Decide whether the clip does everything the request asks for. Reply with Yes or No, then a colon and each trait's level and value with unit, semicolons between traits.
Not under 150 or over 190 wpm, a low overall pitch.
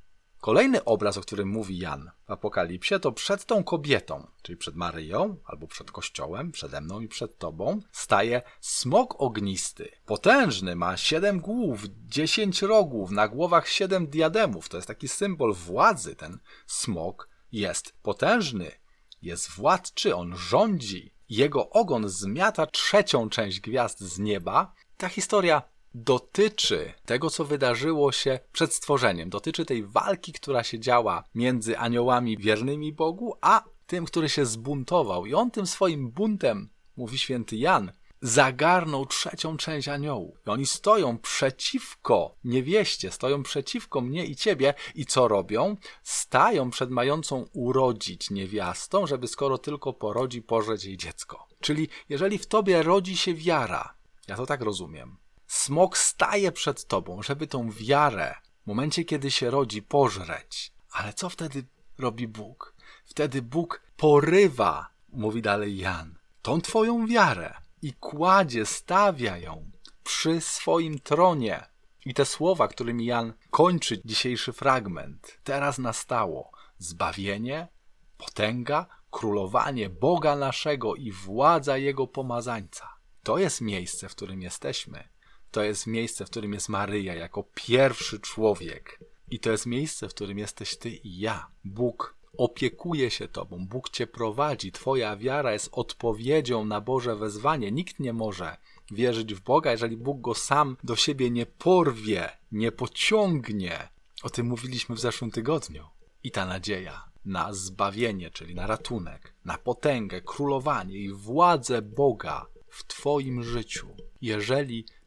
No: average, 135 wpm; low, 125 Hz